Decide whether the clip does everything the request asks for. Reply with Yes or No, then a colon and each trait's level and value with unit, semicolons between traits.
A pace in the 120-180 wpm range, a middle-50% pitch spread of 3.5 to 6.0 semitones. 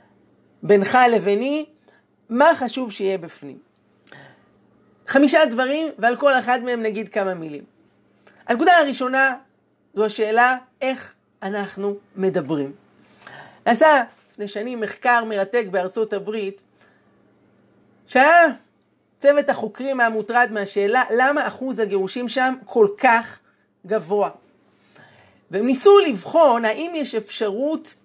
No: slow, 100 wpm; average, 4.5 semitones